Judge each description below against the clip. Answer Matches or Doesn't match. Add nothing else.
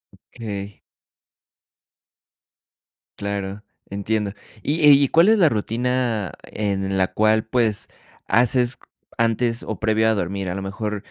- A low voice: Matches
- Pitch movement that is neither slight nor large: Matches